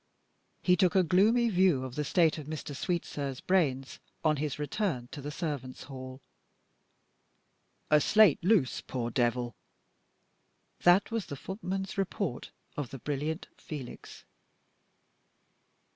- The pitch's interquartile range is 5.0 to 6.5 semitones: Yes, wide, 5.6 semitones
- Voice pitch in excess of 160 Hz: No, medium, 150 Hz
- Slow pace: Yes, slow, 125 wpm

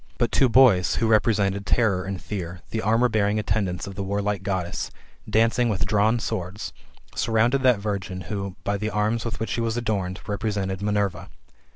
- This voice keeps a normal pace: Yes, average, 175 wpm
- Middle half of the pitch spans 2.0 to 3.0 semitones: Yes, narrow, 2.5 semitones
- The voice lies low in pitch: Yes, low, 105 Hz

